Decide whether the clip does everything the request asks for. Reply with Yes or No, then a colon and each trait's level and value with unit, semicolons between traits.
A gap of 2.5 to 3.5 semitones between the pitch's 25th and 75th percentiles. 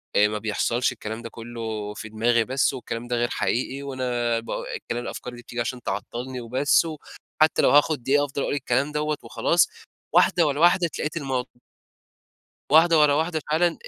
No: average, 4.0 semitones